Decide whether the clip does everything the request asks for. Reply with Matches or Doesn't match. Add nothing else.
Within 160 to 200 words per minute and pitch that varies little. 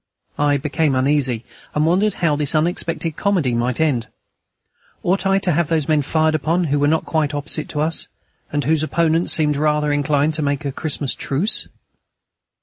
Matches